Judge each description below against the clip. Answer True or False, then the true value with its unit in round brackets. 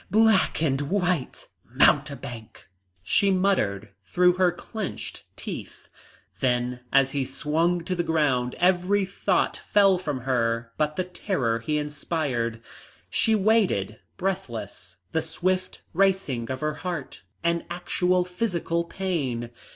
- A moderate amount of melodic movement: False (6.5 semitones)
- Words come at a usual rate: False (120 wpm)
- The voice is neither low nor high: True (165 Hz)